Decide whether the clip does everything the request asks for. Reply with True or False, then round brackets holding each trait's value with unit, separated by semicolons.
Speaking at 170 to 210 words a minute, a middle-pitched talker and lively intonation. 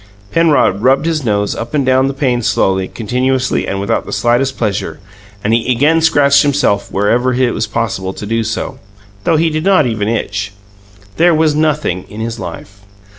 False (180 wpm; 125 Hz; 5.7 semitones)